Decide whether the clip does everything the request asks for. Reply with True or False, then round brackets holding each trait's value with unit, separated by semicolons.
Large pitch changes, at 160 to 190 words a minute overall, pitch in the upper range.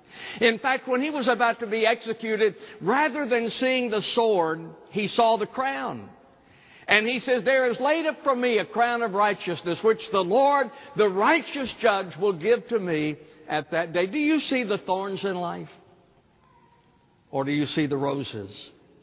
True (6.2 semitones; 180 wpm; 220 Hz)